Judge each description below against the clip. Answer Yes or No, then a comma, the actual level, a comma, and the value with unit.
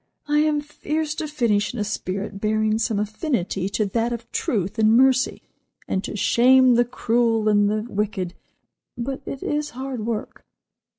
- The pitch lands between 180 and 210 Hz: No, high, 230 Hz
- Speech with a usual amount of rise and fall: Yes, average, 3.8 semitones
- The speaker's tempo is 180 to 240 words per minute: No, average, 165 wpm